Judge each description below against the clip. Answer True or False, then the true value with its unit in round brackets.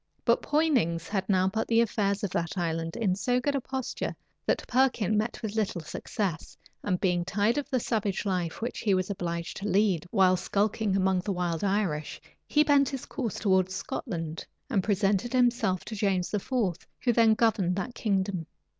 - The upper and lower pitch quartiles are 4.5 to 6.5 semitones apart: False (3.9 semitones)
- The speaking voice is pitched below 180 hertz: False (200 Hz)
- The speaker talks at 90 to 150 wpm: False (180 wpm)